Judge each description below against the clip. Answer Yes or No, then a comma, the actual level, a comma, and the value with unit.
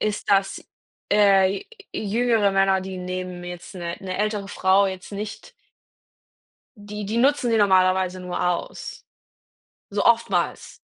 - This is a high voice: Yes, high, 195 Hz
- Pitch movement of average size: No, narrow, 2.1 semitones